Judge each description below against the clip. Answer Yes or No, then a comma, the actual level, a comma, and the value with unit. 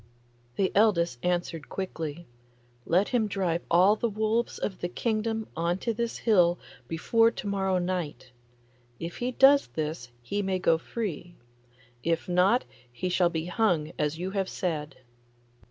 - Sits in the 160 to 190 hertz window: Yes, medium, 185 Hz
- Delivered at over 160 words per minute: No, average, 150 wpm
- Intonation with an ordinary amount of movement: Yes, average, 4.2 semitones